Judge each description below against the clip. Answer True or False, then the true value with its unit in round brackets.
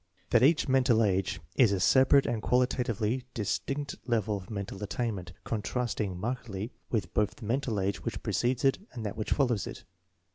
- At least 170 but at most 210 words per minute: True (185 wpm)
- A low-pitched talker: True (115 Hz)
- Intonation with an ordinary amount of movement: True (3.8 semitones)